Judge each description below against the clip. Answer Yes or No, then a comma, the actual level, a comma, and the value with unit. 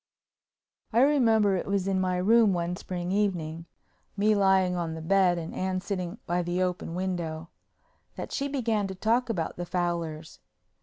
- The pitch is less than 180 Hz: No, medium, 185 Hz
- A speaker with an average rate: Yes, average, 155 wpm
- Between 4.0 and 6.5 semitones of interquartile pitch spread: No, average, 2.8 semitones